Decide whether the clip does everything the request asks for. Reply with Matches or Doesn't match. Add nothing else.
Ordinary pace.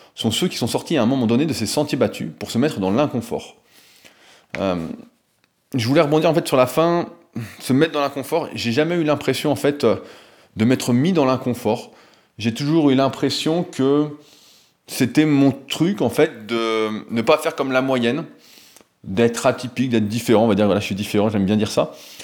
Matches